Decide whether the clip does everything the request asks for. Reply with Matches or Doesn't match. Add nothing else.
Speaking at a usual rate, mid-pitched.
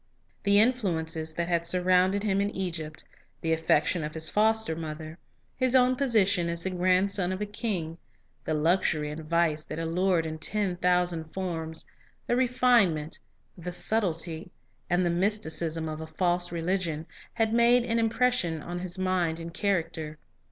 Matches